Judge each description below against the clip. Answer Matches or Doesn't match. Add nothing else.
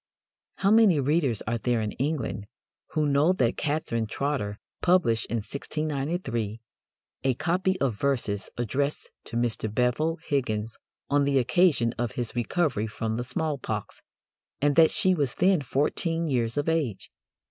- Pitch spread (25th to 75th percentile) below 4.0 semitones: Doesn't match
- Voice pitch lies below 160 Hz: Matches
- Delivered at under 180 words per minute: Matches